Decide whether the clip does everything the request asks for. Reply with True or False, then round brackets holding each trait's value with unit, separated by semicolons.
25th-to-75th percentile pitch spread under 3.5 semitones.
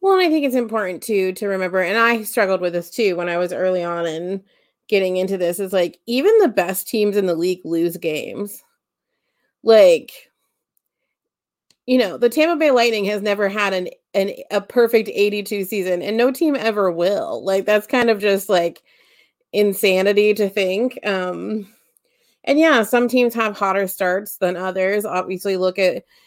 False (4.3 semitones)